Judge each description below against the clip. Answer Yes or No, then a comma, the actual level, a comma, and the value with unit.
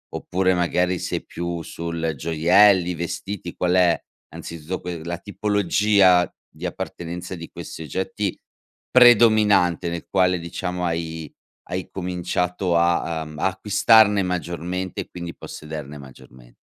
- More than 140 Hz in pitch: No, very low, 90 Hz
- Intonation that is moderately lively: No, narrow, 2.1 semitones